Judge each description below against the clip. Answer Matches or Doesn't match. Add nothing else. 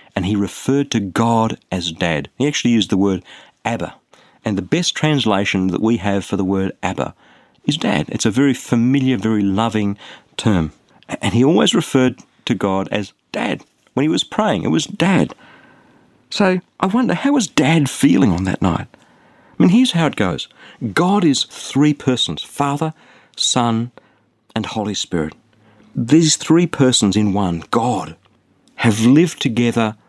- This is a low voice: Matches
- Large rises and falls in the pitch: Matches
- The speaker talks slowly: Doesn't match